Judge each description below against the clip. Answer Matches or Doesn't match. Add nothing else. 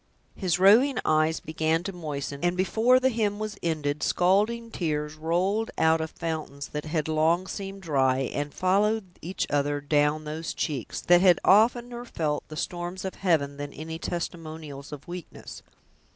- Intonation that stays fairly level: Doesn't match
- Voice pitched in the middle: Matches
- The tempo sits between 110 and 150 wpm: Doesn't match